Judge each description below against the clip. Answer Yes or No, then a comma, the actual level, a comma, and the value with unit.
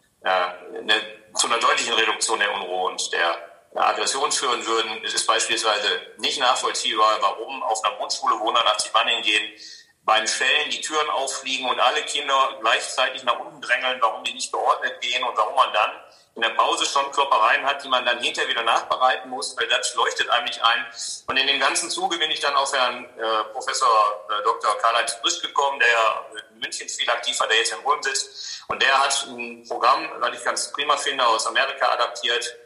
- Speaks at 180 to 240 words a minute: Yes, fast, 190 wpm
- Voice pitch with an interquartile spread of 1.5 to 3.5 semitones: No, average, 4.2 semitones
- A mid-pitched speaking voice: No, low, 120 Hz